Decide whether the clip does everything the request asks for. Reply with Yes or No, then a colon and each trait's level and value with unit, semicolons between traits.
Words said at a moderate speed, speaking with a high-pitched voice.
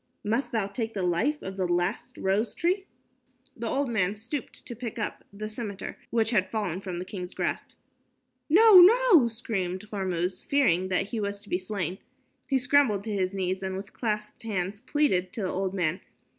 Yes: average, 185 wpm; high, 205 Hz